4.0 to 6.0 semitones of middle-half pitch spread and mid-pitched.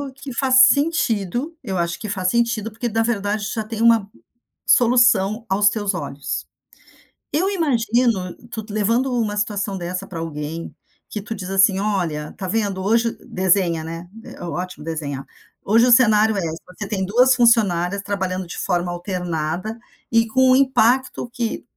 No: average, 4.3 semitones; high, 205 Hz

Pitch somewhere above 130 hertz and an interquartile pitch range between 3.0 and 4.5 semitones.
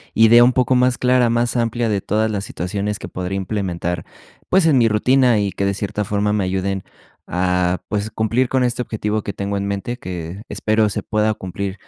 No: low, 105 Hz; average, 3.3 semitones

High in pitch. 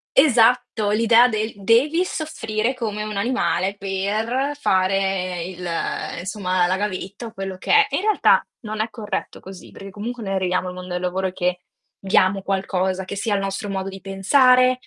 Yes: high, 200 Hz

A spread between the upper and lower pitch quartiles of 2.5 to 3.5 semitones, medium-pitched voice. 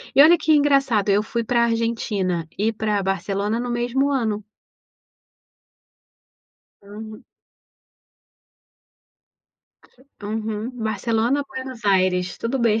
No: average, 3.0 semitones; high, 225 Hz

